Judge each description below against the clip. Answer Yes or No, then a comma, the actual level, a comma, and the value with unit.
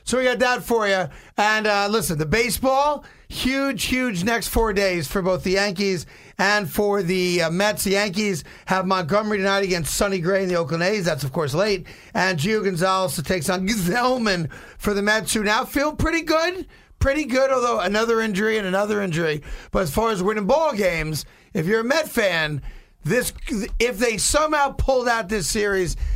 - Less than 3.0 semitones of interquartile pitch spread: No, average, 3.8 semitones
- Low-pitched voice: No, high, 205 Hz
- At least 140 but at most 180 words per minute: No, average, 195 wpm